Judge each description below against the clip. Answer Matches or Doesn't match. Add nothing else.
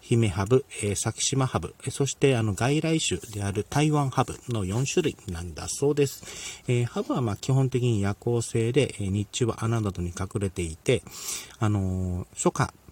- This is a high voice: Doesn't match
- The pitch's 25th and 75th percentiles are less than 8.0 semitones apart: Matches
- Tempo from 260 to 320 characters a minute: Matches